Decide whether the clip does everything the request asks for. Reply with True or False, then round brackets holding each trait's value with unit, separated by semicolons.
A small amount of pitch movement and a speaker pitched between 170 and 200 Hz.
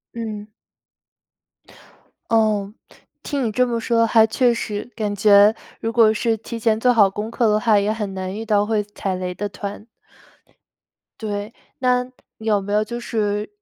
False (1.9 semitones; 215 Hz)